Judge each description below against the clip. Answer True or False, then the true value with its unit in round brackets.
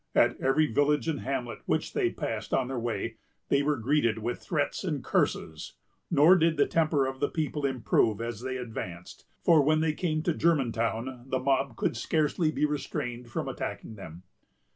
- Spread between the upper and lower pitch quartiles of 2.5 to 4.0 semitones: False (4.4 semitones)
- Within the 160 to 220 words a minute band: True (180 wpm)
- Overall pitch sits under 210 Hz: True (135 Hz)